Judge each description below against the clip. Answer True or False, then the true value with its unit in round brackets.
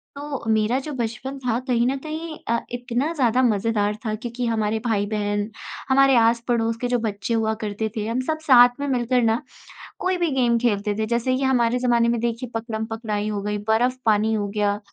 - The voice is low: False (235 Hz)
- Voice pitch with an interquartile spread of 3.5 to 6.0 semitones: False (2.6 semitones)